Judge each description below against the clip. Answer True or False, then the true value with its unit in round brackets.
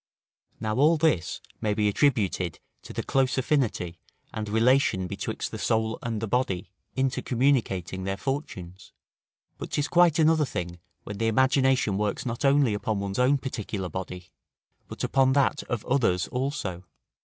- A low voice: True (115 Hz)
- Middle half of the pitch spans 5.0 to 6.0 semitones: True (5.6 semitones)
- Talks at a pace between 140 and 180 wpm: True (150 wpm)